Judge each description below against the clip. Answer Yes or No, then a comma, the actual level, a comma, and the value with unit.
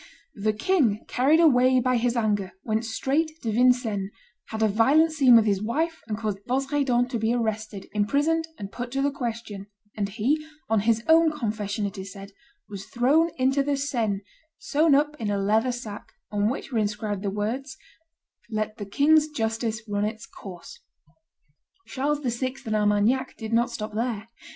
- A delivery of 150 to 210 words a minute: Yes, average, 175 wpm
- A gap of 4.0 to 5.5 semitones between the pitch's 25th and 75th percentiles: Yes, average, 4.5 semitones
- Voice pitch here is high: Yes, high, 230 Hz